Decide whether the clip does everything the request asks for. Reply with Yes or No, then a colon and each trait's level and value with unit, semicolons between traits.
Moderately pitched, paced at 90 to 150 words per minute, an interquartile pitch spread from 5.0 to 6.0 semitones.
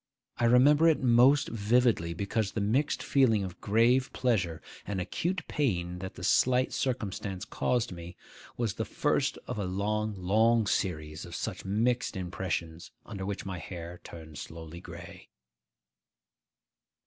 No: low, 105 Hz; average, 140 wpm; wide, 5.4 semitones